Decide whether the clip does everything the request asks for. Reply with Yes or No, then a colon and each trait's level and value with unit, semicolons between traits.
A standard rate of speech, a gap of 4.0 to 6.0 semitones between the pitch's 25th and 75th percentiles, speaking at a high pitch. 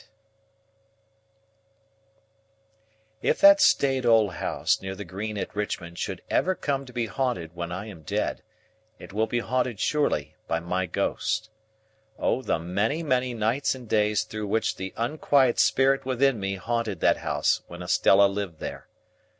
No: average, 150 wpm; average, 5.1 semitones; low, 110 Hz